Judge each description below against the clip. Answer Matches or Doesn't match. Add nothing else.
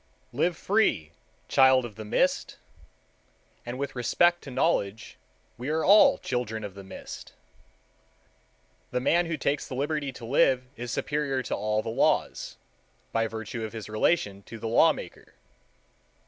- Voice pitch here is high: Doesn't match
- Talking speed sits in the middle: Matches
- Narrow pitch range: Doesn't match